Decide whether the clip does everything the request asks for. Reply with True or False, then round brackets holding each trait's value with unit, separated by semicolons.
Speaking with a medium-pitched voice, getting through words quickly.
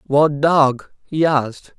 False (145 Hz; 135 wpm)